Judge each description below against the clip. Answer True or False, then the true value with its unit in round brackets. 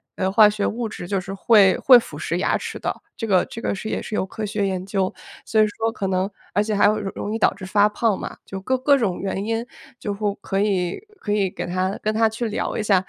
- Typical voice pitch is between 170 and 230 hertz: True (205 Hz)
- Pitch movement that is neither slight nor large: False (2.2 semitones)